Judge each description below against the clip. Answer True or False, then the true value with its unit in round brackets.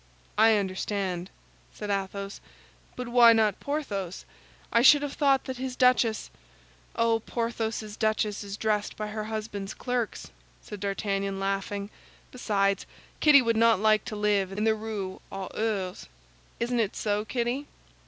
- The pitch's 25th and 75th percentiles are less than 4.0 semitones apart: True (2.8 semitones)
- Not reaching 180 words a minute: True (145 wpm)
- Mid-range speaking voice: False (215 Hz)